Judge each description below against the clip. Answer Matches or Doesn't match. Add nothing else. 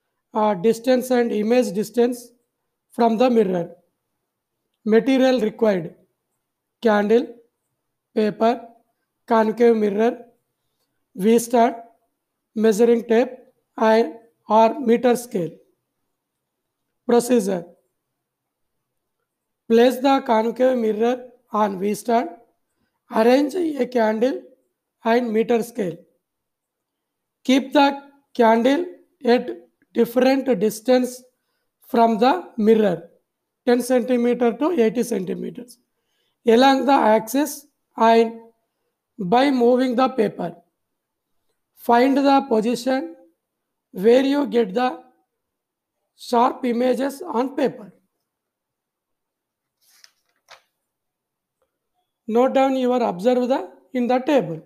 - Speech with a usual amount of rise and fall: Doesn't match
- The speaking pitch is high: Matches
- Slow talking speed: Matches